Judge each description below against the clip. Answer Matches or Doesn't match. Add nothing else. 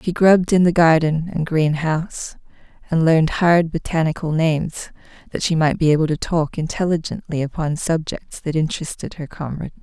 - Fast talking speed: Doesn't match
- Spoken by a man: Doesn't match